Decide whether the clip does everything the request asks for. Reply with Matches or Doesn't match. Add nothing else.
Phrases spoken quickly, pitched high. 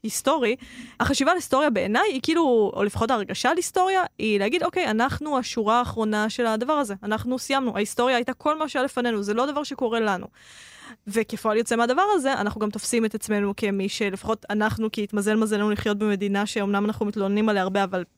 Matches